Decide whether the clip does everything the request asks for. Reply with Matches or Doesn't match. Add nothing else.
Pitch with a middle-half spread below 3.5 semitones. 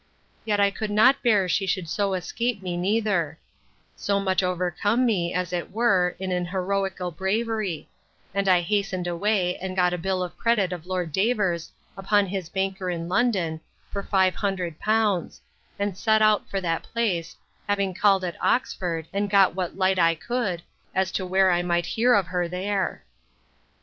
Matches